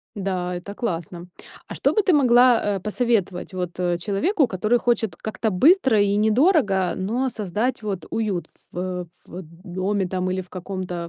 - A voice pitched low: No, high, 200 Hz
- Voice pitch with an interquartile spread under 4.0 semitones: No, average, 4.3 semitones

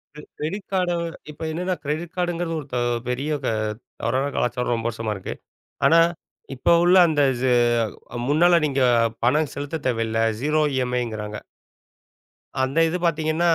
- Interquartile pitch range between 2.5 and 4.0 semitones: No, average, 5.0 semitones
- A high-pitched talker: No, medium, 145 Hz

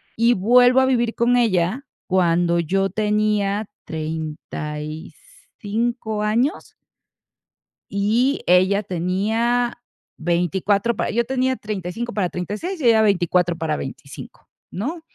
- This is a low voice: No, high, 205 Hz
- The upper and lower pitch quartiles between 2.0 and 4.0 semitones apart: No, average, 5.0 semitones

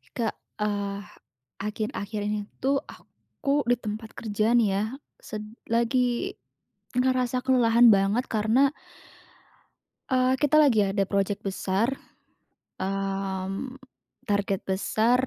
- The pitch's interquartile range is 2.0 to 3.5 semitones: No, average, 3.9 semitones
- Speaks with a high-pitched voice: Yes, high, 215 Hz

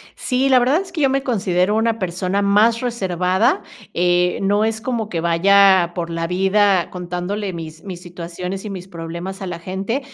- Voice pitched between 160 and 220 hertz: Yes, high, 190 Hz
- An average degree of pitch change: Yes, average, 3.7 semitones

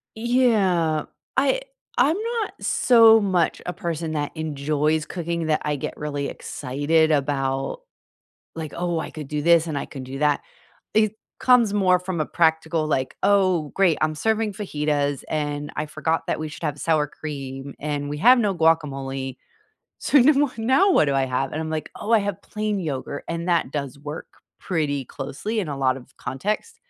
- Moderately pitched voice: Yes, medium, 160 Hz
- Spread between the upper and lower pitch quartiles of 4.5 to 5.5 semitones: Yes, average, 5.1 semitones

